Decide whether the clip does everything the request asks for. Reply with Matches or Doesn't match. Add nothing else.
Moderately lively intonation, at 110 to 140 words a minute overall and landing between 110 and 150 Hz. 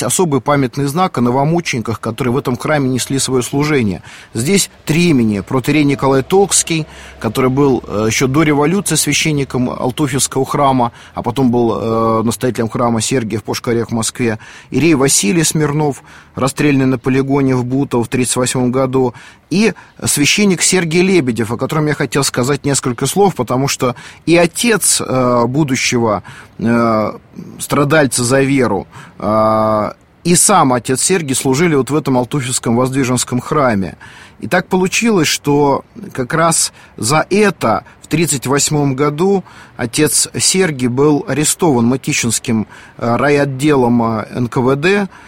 Matches